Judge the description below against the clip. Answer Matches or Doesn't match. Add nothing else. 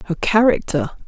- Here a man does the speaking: Doesn't match